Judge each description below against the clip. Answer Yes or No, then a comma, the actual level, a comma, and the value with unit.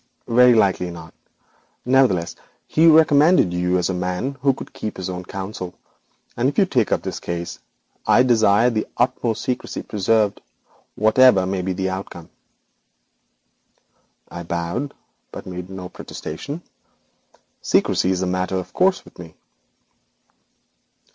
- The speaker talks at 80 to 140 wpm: Yes, slow, 135 wpm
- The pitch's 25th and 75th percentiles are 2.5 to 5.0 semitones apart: No, wide, 5.6 semitones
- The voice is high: No, very low, 95 Hz